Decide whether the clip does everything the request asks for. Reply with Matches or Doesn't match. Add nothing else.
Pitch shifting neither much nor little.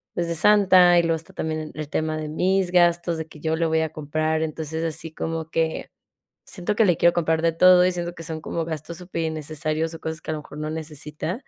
Doesn't match